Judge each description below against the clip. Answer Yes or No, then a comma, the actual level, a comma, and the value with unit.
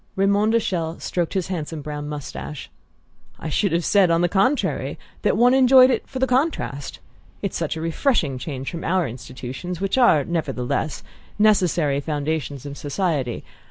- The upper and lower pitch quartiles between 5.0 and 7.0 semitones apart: Yes, wide, 5.4 semitones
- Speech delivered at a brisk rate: No, average, 165 wpm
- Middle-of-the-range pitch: Yes, medium, 165 Hz